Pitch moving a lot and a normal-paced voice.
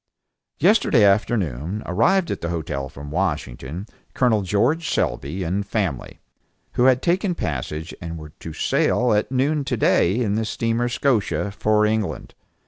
Yes: wide, 6.9 semitones; average, 145 wpm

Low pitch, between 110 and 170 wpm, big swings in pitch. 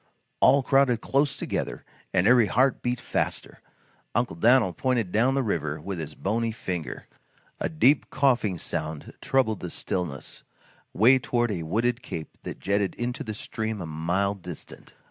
Yes: low, 110 Hz; average, 155 wpm; wide, 5.9 semitones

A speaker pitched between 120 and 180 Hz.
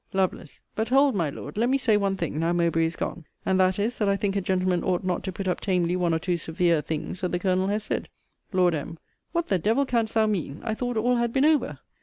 No: high, 190 Hz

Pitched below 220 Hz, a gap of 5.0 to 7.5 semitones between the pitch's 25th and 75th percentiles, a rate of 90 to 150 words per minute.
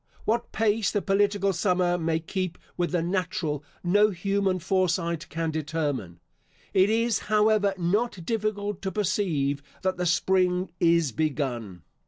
No: medium, 185 Hz; average, 3.8 semitones; slow, 135 wpm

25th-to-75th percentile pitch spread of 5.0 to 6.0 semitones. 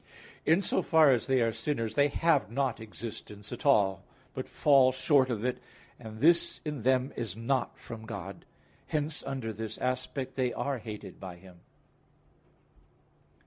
No: average, 4.0 semitones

